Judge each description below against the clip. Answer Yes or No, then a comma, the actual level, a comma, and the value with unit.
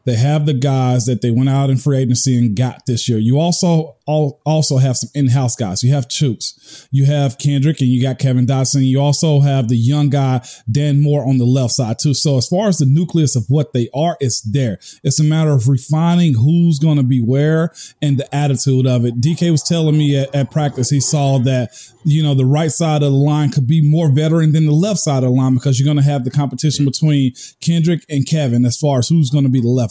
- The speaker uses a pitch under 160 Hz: Yes, medium, 140 Hz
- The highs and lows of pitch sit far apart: No, average, 2.8 semitones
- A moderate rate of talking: No, fast, 250 wpm